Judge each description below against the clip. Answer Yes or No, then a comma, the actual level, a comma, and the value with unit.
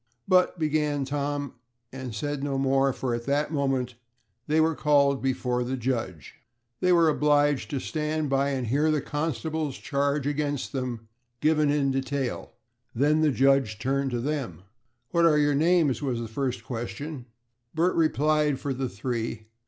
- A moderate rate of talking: Yes, average, 160 wpm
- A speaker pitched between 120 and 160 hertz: Yes, medium, 140 Hz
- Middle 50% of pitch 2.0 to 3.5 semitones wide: Yes, average, 2.7 semitones